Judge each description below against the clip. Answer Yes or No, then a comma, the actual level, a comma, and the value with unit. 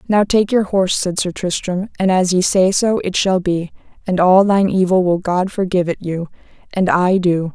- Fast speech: Yes, fast, 215 wpm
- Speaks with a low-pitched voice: No, medium, 185 Hz